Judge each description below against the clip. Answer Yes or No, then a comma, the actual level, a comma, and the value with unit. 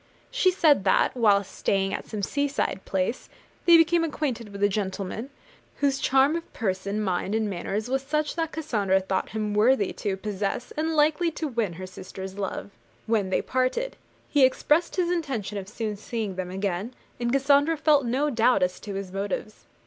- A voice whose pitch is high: Yes, high, 225 Hz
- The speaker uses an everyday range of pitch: No, wide, 6.6 semitones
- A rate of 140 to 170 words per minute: No, average, 180 wpm